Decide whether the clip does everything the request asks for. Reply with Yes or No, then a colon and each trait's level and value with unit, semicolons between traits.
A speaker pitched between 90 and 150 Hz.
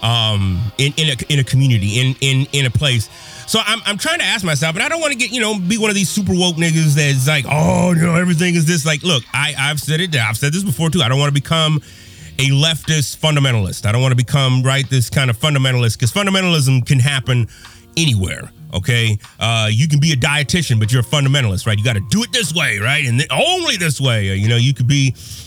Yes: medium, 140 Hz